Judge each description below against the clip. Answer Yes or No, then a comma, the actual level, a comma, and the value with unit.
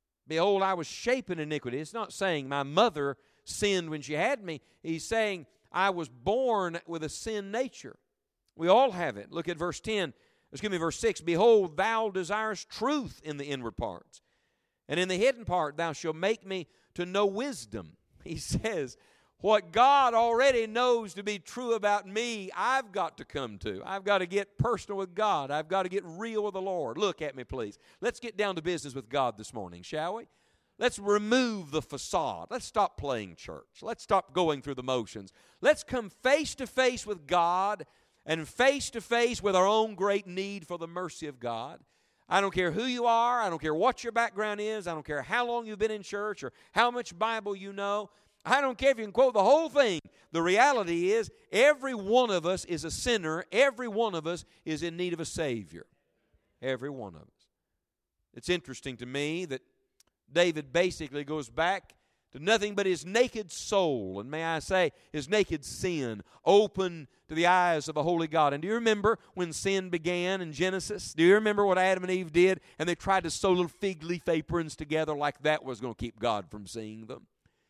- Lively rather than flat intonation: Yes, wide, 5.7 semitones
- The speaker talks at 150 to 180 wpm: No, fast, 205 wpm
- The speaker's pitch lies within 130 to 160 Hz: No, medium, 185 Hz